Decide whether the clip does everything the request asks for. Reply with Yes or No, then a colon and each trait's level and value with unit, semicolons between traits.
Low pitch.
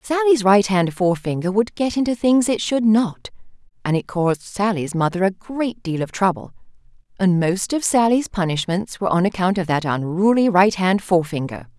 No: high, 195 Hz